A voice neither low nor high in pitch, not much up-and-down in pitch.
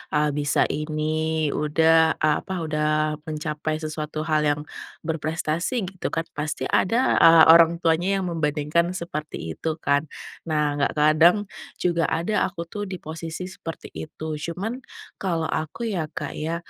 Yes: medium, 160 Hz; narrow, 1.9 semitones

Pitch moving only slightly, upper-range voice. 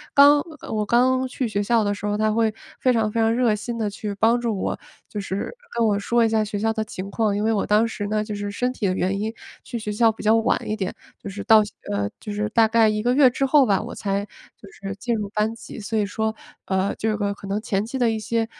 Yes: narrow, 2.0 semitones; high, 215 Hz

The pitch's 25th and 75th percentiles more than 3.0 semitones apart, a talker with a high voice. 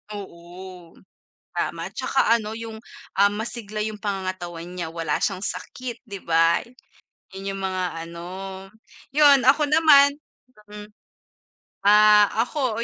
Yes: average, 4.3 semitones; high, 205 Hz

